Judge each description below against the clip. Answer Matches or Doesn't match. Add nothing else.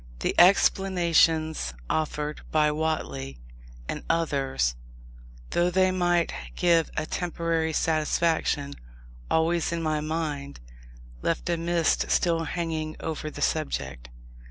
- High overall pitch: Doesn't match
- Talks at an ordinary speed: Doesn't match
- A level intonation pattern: Matches